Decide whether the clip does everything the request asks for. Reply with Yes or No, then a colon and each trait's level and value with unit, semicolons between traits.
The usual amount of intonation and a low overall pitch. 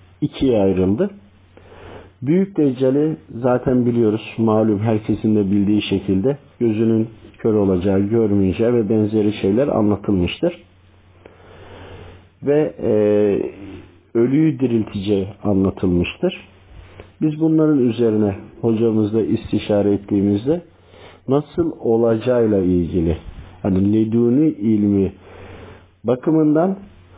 Yes: average, 3.4 semitones; low, 105 Hz